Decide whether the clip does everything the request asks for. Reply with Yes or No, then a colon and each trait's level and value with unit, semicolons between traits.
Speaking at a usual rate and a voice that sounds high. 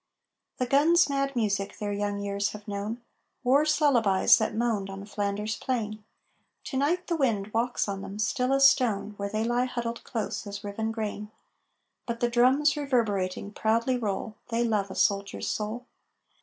Yes: average, 165 wpm; high, 220 Hz